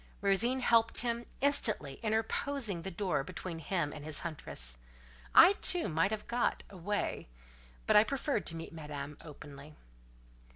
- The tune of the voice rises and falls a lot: Yes, wide, 7.3 semitones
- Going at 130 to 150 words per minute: Yes, average, 140 wpm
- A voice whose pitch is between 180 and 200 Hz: Yes, high, 190 Hz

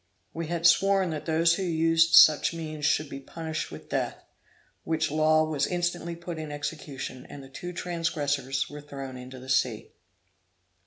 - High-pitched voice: No, medium, 155 Hz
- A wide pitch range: No, average, 2.9 semitones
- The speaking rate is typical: Yes, average, 165 wpm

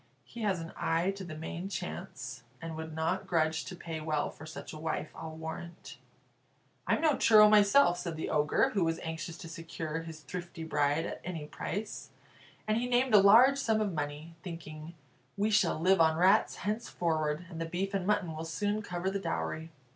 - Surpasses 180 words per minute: Yes, average, 190 wpm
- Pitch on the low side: No, medium, 170 Hz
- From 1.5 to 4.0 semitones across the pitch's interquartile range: Yes, average, 3.7 semitones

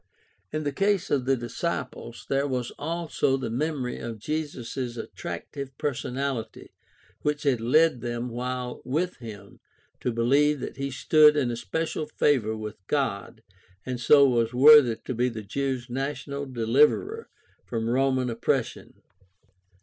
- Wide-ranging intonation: No, average, 3.7 semitones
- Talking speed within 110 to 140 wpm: Yes, slow, 135 wpm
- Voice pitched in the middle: No, low, 130 Hz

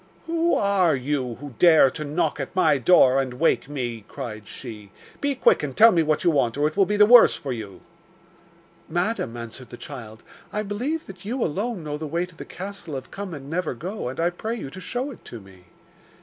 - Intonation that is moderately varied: No, wide, 7.5 semitones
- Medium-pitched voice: Yes, medium, 155 Hz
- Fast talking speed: Yes, fast, 220 wpm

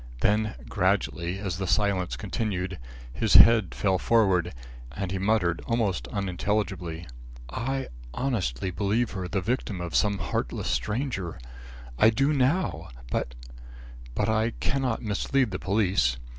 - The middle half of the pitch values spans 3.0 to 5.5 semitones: Yes, average, 3.7 semitones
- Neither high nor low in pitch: No, low, 100 Hz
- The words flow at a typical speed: No, slow, 130 wpm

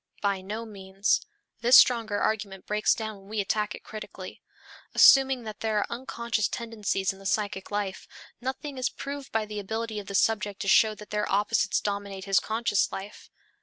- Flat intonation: Yes, narrow, 2.1 semitones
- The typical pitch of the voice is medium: No, high, 210 Hz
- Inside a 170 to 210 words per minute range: Yes, average, 180 wpm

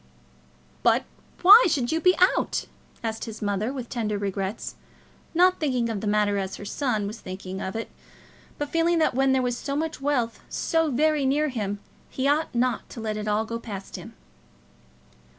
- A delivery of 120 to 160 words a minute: No, average, 185 wpm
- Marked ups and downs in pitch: Yes, wide, 5.7 semitones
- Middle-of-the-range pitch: No, high, 240 Hz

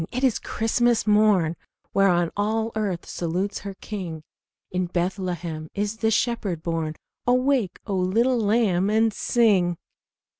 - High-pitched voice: Yes, high, 200 Hz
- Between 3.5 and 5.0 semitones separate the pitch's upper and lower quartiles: Yes, average, 4.1 semitones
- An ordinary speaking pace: No, slow, 120 wpm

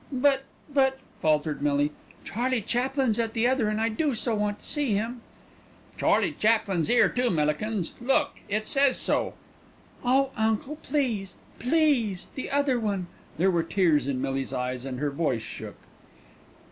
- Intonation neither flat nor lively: No, wide, 7.5 semitones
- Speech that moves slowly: No, average, 160 wpm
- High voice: Yes, high, 220 Hz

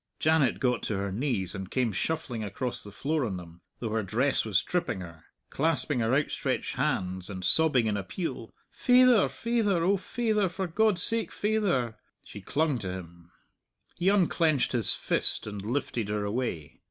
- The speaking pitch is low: Yes, low, 125 Hz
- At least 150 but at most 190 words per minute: Yes, average, 165 wpm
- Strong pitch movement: Yes, wide, 8.3 semitones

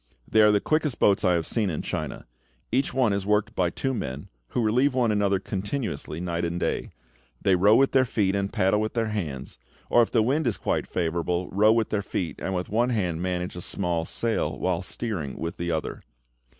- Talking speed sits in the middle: No, fast, 215 wpm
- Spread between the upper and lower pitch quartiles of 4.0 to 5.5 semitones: Yes, average, 4.4 semitones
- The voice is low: Yes, low, 100 Hz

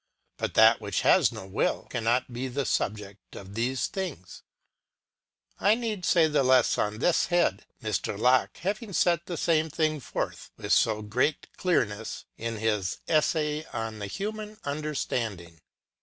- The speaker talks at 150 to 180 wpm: Yes, average, 155 wpm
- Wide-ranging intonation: Yes, wide, 7.4 semitones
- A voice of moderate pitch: No, low, 130 Hz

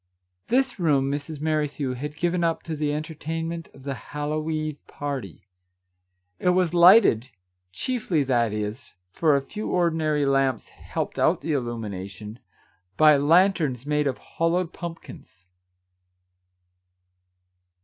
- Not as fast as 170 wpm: Yes, slow, 135 wpm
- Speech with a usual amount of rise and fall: Yes, average, 4.1 semitones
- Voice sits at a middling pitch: Yes, medium, 150 Hz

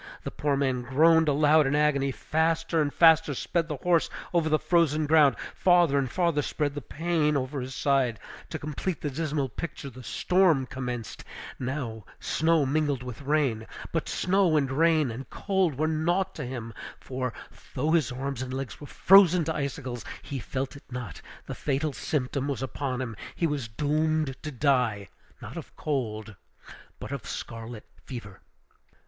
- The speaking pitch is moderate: Yes, medium, 145 Hz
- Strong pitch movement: No, average, 3.6 semitones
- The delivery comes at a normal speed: Yes, average, 165 wpm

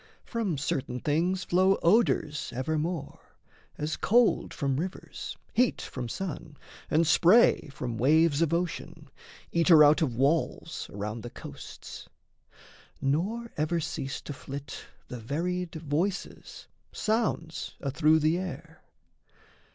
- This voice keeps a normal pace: No, slow, 115 wpm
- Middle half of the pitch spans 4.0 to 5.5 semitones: Yes, average, 4.3 semitones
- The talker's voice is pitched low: No, medium, 160 Hz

